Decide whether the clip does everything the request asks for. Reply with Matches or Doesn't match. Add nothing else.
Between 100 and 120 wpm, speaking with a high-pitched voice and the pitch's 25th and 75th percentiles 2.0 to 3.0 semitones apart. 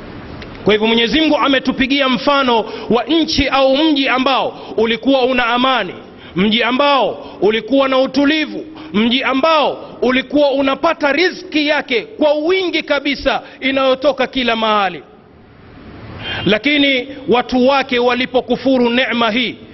Matches